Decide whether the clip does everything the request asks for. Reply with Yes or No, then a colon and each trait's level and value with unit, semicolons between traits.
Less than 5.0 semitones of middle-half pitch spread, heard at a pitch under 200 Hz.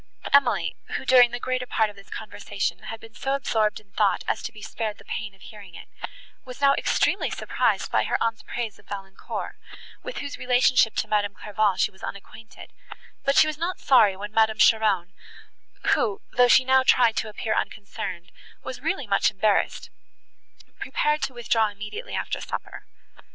No: average, 3.7 semitones; high, 220 Hz